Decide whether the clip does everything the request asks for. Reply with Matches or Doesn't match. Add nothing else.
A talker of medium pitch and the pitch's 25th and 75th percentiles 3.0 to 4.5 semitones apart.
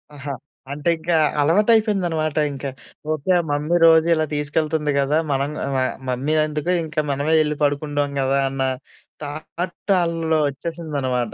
Doesn't match